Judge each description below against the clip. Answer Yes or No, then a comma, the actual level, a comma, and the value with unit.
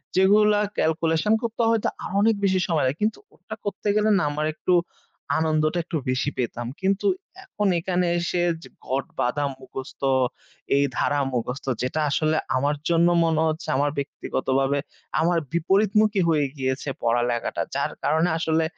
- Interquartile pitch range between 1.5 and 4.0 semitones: No, average, 5.2 semitones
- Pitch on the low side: No, medium, 160 Hz